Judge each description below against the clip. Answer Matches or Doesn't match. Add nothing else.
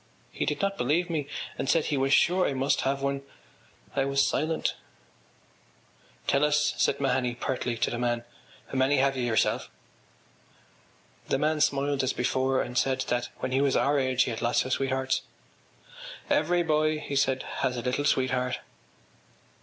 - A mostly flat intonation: Matches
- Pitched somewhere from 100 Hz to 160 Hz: Matches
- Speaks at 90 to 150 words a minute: Doesn't match